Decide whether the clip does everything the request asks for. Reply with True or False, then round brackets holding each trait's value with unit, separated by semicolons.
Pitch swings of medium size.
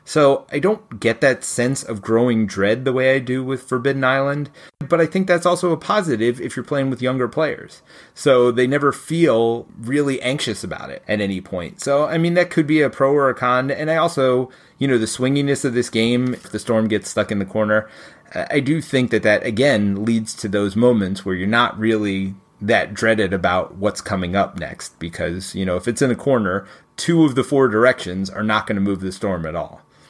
True (4.6 semitones)